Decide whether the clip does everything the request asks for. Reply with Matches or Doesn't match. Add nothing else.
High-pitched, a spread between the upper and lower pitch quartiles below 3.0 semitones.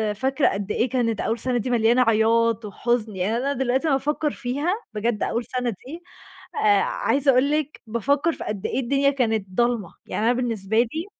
Doesn't match